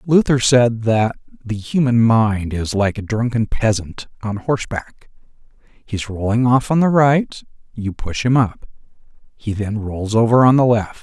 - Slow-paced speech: No, average, 170 wpm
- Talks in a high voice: No, low, 115 Hz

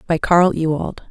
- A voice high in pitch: No, medium, 165 Hz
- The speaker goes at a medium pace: Yes, average, 165 wpm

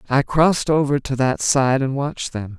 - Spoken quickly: Yes, fast, 210 wpm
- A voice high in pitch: No, low, 135 Hz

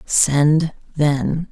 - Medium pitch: Yes, medium, 150 Hz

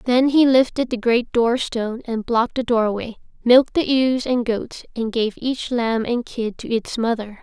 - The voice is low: No, high, 235 Hz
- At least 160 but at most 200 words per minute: Yes, average, 195 wpm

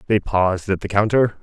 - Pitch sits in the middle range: No, low, 100 Hz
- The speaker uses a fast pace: Yes, fast, 210 wpm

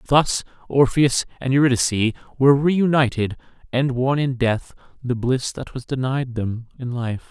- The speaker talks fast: No, average, 155 wpm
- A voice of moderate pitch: No, low, 130 Hz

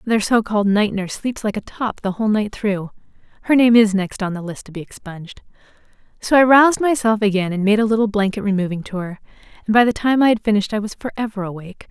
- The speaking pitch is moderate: No, high, 210 Hz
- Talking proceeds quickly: Yes, fast, 225 wpm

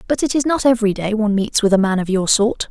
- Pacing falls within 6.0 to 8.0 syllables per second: Yes, 6.7 syllables/s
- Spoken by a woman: Yes, female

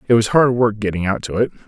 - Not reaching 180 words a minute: No, fast, 285 wpm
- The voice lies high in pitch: No, low, 110 Hz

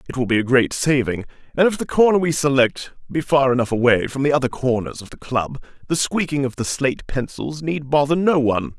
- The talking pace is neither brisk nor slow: No, fast, 225 wpm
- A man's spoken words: Yes, male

